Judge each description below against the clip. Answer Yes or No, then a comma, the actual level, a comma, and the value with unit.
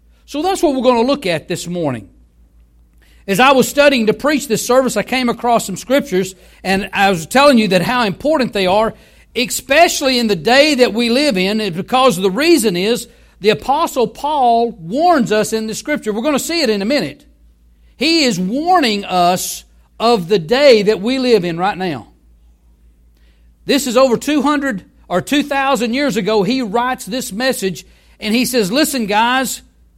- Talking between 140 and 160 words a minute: No, average, 180 wpm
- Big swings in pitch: Yes, wide, 6.0 semitones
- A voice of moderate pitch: No, high, 225 Hz